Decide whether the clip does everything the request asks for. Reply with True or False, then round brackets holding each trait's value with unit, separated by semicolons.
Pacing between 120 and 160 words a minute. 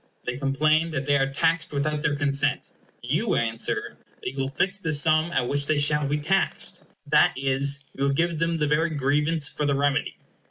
False (195 wpm)